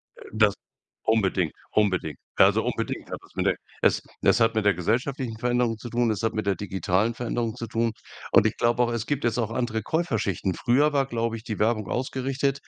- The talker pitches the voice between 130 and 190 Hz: No, low, 115 Hz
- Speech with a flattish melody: Yes, narrow, 2.3 semitones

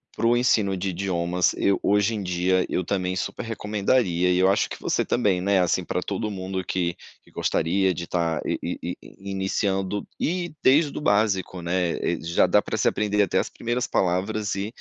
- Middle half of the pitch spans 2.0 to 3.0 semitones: Yes, narrow, 2.5 semitones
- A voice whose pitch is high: No, very low, 95 Hz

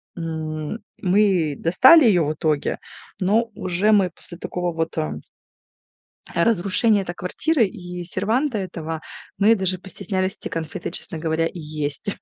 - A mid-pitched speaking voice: Yes, medium, 180 Hz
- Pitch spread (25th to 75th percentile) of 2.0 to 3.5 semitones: No, average, 3.9 semitones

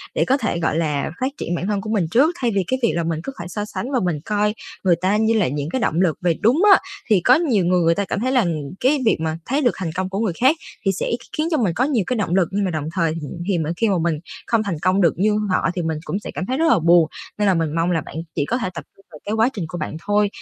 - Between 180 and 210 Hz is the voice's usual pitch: Yes, high, 195 Hz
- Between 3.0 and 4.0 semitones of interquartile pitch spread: No, average, 5.1 semitones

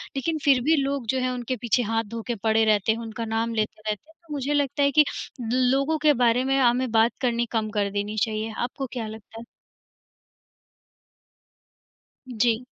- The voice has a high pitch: Yes, high, 240 Hz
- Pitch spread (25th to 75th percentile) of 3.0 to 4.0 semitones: Yes, average, 3.3 semitones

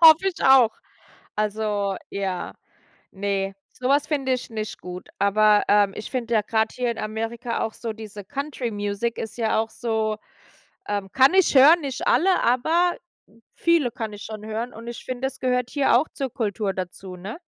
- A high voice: Yes, high, 225 Hz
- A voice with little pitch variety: No, average, 4.1 semitones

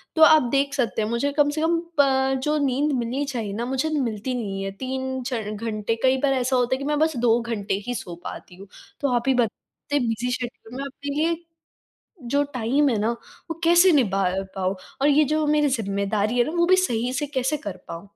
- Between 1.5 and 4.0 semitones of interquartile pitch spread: No, average, 4.4 semitones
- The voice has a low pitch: No, very high, 255 Hz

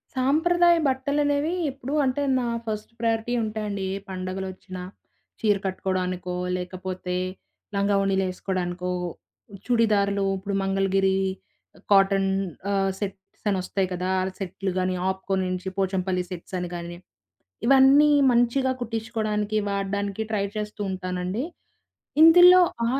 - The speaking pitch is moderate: No, high, 195 Hz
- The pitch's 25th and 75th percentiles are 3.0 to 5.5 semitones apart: Yes, average, 3.7 semitones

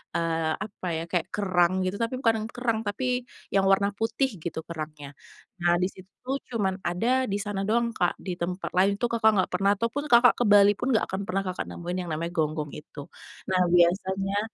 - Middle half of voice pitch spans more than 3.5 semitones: Yes, average, 4.1 semitones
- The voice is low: No, high, 195 Hz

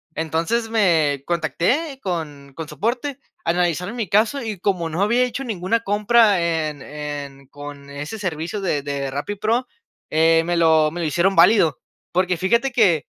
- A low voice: No, medium, 175 Hz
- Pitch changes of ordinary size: No, wide, 5.8 semitones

